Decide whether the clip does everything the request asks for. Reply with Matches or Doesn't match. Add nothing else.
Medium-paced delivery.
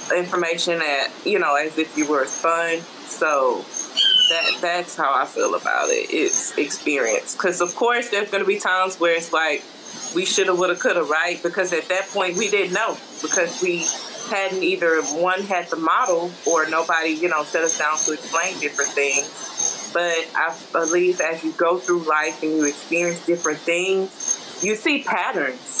Matches